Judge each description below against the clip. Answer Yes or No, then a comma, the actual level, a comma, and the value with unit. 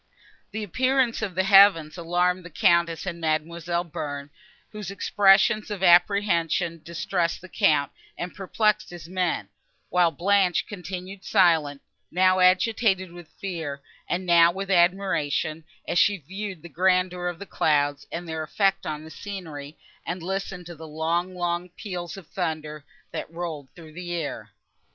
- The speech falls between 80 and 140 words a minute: No, average, 150 wpm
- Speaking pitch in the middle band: Yes, medium, 175 Hz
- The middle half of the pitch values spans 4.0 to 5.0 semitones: No, average, 2.8 semitones